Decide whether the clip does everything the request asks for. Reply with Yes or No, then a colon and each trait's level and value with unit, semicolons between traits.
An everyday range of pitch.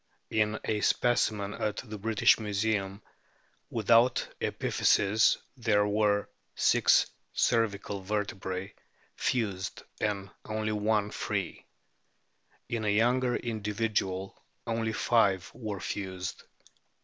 No: narrow, 1.8 semitones